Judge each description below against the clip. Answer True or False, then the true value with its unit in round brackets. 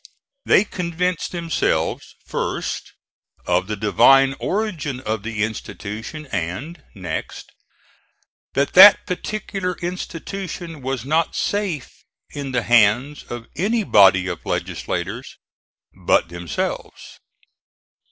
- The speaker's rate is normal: False (100 wpm)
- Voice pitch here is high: False (135 Hz)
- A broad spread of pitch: True (8.7 semitones)